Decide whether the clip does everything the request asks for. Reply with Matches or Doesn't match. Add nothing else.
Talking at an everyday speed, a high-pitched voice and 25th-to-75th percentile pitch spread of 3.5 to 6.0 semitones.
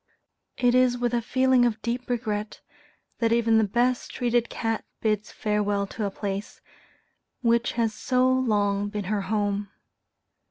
Doesn't match